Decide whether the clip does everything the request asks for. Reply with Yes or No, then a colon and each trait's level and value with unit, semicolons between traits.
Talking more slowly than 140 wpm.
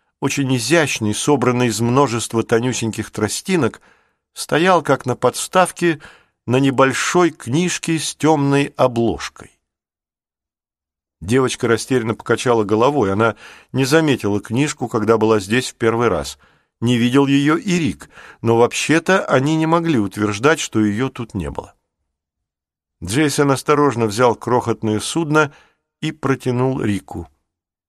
Yes: average, 120 wpm